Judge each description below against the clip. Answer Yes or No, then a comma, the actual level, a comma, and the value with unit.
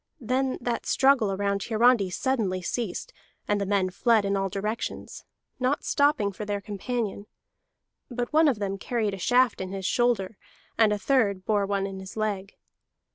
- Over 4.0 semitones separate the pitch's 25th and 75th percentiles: No, average, 3.7 semitones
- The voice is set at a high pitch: Yes, high, 210 Hz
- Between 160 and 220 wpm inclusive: Yes, average, 170 wpm